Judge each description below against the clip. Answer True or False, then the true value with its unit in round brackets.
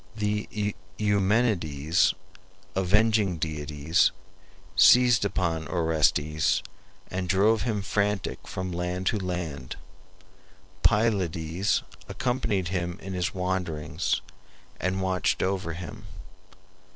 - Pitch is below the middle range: True (95 Hz)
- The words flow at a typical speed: False (90 wpm)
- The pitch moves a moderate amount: True (3.7 semitones)